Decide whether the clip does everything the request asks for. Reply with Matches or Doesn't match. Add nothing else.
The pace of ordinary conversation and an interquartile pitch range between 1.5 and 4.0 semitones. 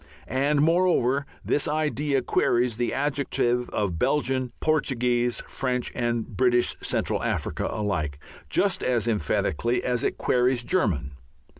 Doesn't match